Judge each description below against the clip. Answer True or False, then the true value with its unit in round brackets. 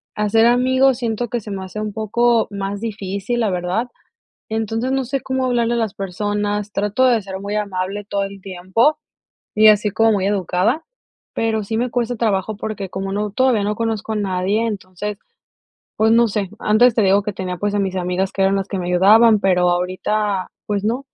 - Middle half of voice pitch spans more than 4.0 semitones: False (2.7 semitones)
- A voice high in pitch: True (210 Hz)